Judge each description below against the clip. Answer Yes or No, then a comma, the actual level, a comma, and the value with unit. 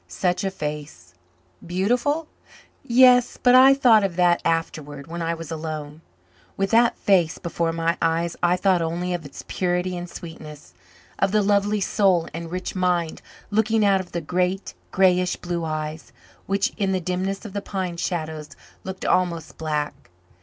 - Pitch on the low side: No, medium, 180 Hz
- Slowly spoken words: No, average, 160 wpm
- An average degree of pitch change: Yes, average, 3.1 semitones